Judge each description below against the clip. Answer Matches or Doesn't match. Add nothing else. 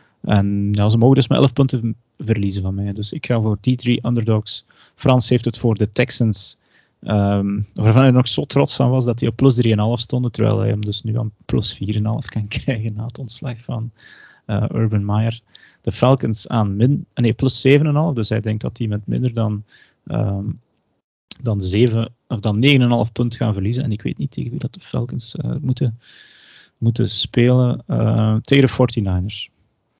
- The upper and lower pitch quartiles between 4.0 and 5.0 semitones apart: Doesn't match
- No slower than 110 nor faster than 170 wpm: Doesn't match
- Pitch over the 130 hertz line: Doesn't match